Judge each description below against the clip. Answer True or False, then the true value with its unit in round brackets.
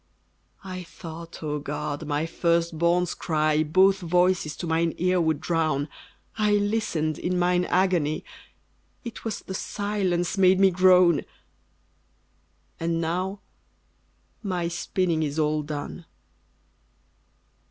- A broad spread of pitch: False (2.8 semitones)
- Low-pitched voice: False (170 Hz)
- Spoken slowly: True (115 wpm)